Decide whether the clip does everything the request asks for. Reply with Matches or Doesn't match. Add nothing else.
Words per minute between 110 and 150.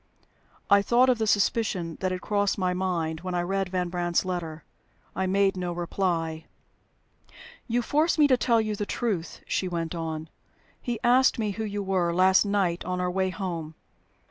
Doesn't match